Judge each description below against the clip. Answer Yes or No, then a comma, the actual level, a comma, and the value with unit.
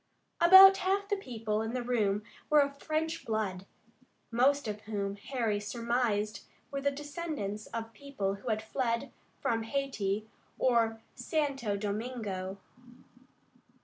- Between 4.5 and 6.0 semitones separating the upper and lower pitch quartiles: Yes, average, 5.0 semitones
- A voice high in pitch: Yes, high, 230 Hz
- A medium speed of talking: No, slow, 120 wpm